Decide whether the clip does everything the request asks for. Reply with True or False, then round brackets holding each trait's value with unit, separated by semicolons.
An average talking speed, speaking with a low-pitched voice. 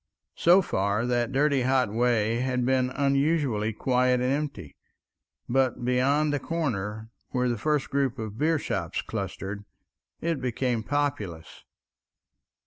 False (125 wpm; 125 Hz)